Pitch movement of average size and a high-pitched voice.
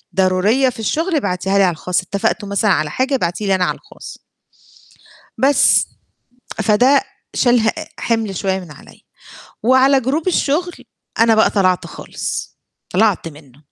No: wide, 6.0 semitones; high, 210 Hz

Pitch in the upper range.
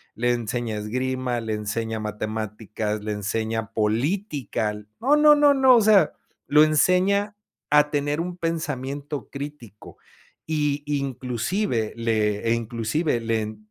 No: low, 125 Hz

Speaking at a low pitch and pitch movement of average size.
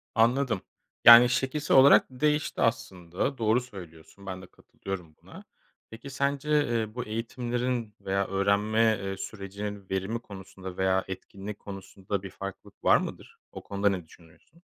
Yes: low, 105 Hz; average, 4.1 semitones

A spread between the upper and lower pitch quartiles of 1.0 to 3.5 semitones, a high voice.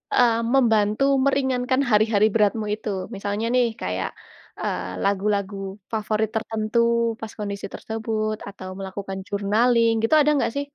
Yes: narrow, 2.4 semitones; high, 215 Hz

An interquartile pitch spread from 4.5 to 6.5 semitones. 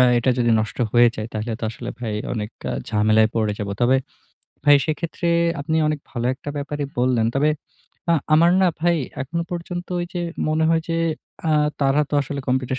Yes: average, 5.1 semitones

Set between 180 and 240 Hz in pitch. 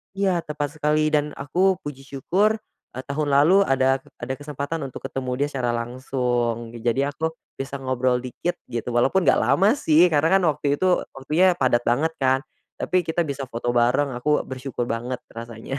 No: medium, 140 Hz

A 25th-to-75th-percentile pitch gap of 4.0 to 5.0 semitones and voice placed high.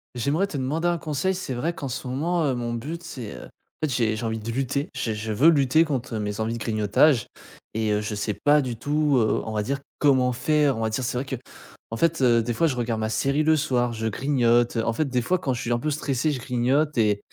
No: average, 4.5 semitones; low, 125 Hz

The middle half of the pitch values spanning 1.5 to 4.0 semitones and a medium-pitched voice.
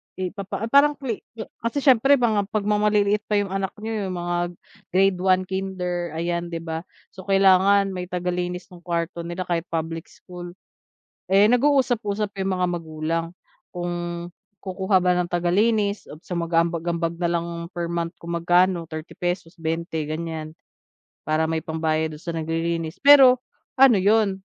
Yes: average, 3.2 semitones; medium, 180 Hz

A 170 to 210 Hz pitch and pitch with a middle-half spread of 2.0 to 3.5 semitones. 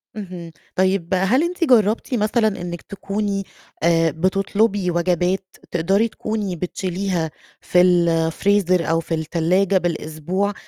Yes: medium, 185 Hz; average, 2.9 semitones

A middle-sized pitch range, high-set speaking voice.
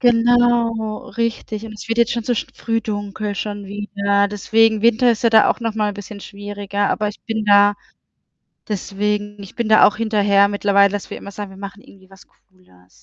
No: narrow, 1.9 semitones; high, 210 Hz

